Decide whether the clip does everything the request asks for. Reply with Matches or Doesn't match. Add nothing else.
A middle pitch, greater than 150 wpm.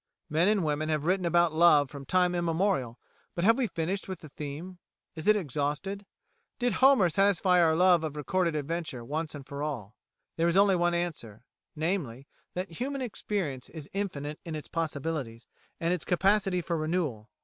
Matches